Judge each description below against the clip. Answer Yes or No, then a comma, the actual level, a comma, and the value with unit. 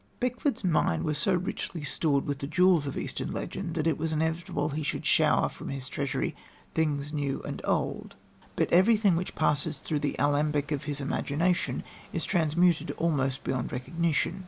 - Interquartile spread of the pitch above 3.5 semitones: No, average, 3.1 semitones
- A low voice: No, medium, 155 Hz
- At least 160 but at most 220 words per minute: Yes, average, 170 wpm